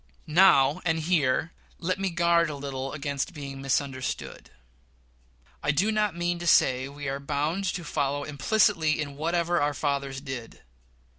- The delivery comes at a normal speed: Yes, average, 150 wpm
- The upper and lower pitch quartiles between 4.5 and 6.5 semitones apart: No, average, 3.7 semitones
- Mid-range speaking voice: Yes, medium, 150 Hz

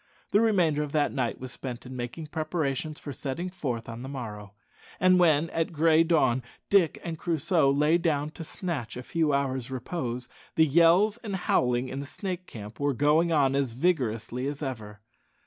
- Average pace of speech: Yes, average, 180 wpm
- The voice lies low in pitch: No, medium, 145 Hz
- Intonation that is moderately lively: Yes, average, 4.7 semitones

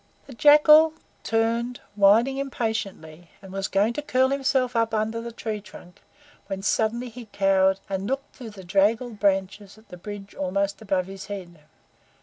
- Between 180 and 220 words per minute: No, average, 165 wpm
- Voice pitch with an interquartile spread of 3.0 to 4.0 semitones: Yes, average, 3.6 semitones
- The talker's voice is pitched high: Yes, high, 215 Hz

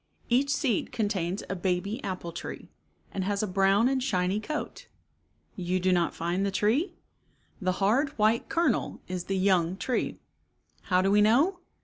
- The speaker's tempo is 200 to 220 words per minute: No, average, 160 wpm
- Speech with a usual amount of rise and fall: Yes, average, 4.1 semitones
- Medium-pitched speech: No, high, 200 Hz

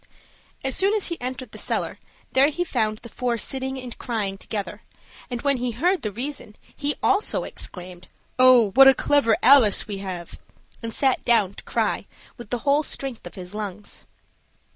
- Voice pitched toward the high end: Yes, high, 245 Hz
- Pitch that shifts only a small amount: No, average, 4.6 semitones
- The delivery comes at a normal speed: Yes, average, 180 wpm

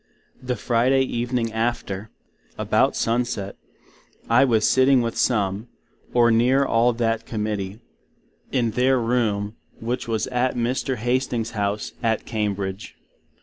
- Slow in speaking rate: Yes, slow, 125 wpm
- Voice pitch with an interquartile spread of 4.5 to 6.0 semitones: No, narrow, 2.5 semitones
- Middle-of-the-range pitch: No, low, 115 Hz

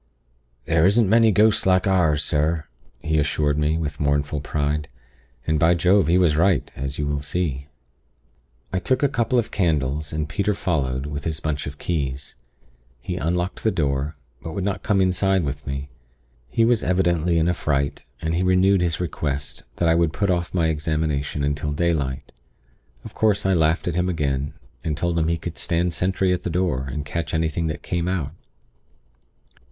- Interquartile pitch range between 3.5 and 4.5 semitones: Yes, average, 3.8 semitones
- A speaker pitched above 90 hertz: No, very low, 80 Hz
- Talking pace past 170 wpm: Yes, average, 185 wpm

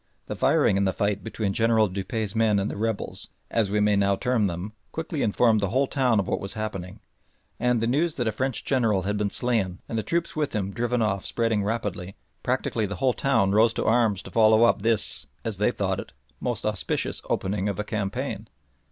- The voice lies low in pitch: Yes, low, 110 Hz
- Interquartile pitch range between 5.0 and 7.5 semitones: No, average, 2.9 semitones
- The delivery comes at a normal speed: No, fast, 215 wpm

